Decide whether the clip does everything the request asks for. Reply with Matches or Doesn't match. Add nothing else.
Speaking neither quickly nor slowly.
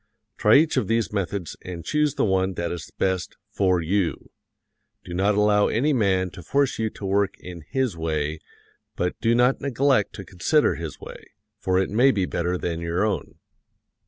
Matches